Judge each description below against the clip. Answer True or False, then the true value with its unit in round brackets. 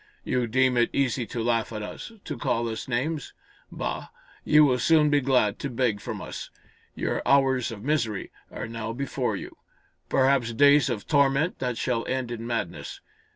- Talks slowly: False (175 wpm)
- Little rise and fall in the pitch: False (3.2 semitones)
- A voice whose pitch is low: True (125 Hz)